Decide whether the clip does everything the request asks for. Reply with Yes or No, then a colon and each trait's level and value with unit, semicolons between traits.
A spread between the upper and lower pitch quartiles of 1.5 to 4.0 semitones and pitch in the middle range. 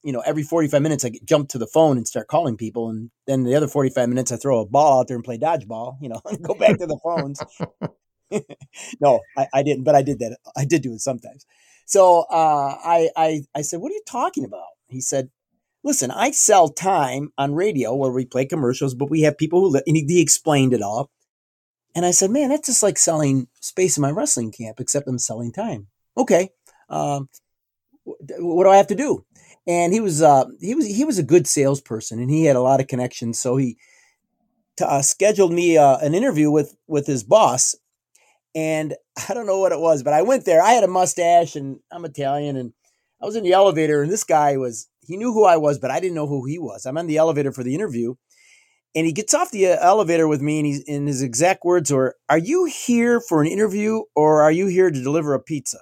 No: average, 5.1 semitones; medium, 150 Hz